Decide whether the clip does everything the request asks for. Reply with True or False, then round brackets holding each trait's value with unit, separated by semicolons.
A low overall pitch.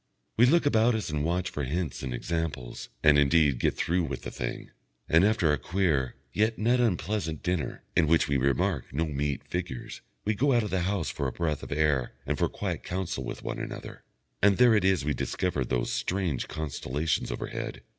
True (80 Hz)